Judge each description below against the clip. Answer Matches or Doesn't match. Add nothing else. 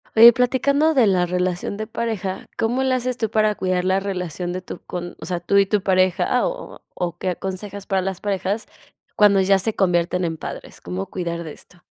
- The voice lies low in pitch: Doesn't match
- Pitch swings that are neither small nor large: Matches